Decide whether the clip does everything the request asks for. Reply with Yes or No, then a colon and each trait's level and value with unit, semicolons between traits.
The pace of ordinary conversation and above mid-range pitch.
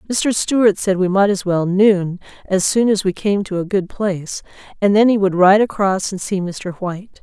No: fast, 225 wpm; high, 195 Hz